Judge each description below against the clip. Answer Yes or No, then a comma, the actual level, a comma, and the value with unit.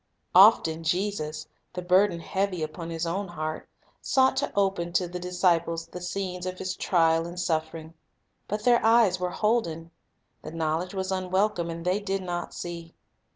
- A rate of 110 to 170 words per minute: Yes, average, 165 wpm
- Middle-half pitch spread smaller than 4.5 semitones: Yes, narrow, 2.4 semitones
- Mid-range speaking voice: Yes, medium, 180 Hz